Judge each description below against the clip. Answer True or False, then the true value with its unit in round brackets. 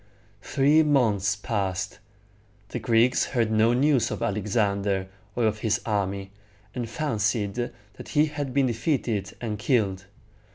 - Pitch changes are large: False (3.8 semitones)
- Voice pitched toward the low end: True (110 Hz)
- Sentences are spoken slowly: True (130 wpm)